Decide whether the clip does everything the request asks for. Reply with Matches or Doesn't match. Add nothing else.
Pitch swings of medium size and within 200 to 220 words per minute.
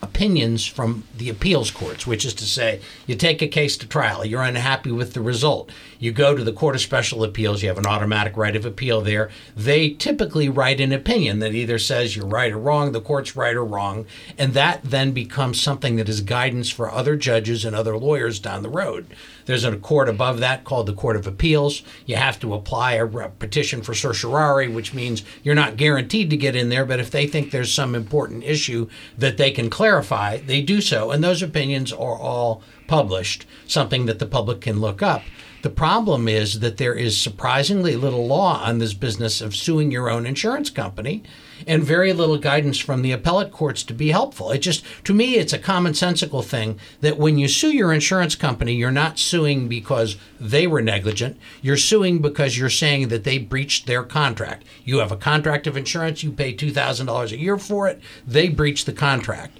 Matches